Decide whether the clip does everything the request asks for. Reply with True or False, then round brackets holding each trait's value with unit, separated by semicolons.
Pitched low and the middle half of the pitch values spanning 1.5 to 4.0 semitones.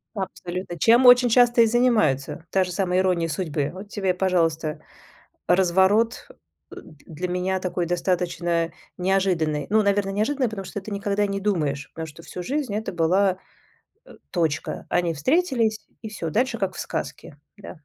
False (190 Hz; 3.7 semitones)